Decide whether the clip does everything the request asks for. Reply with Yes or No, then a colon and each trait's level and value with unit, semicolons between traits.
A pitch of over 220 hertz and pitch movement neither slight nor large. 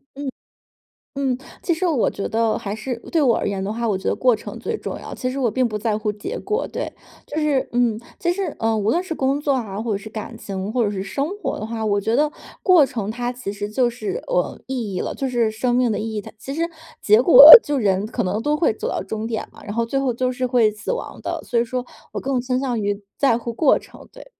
Yes: high, 240 Hz; average, 4.2 semitones